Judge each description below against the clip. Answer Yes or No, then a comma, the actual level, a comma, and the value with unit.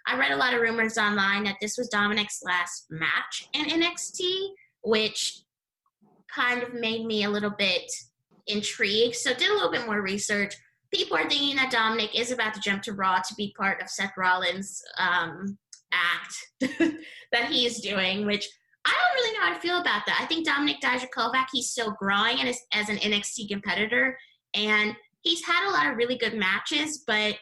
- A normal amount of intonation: Yes, average, 4.7 semitones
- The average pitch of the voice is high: Yes, high, 225 Hz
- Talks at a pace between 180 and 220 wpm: Yes, average, 185 wpm